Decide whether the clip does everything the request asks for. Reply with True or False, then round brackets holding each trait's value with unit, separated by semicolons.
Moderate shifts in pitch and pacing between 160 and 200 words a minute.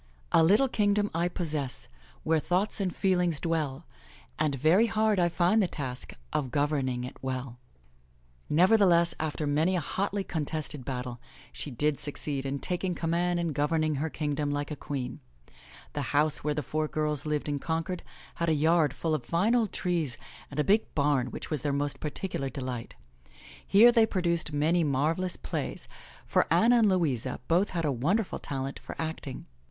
True (3.8 semitones; 170 wpm)